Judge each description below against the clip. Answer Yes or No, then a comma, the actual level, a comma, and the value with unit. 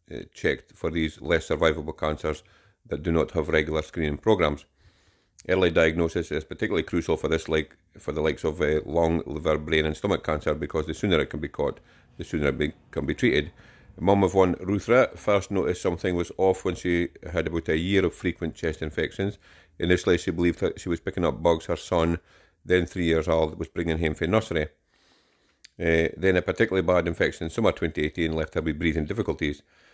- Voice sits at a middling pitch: No, very low, 85 Hz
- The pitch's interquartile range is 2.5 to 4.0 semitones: Yes, average, 2.8 semitones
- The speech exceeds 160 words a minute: Yes, average, 200 wpm